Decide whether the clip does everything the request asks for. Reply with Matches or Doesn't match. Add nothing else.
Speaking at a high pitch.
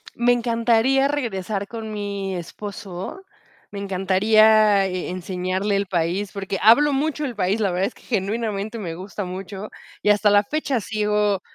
Matches